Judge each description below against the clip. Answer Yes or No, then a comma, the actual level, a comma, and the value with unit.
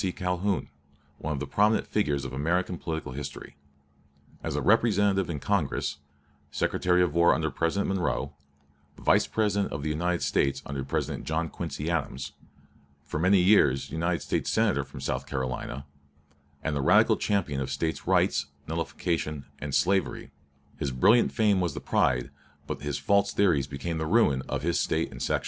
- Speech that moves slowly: No, average, 160 wpm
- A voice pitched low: Yes, very low, 80 Hz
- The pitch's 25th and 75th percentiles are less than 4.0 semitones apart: No, average, 5.0 semitones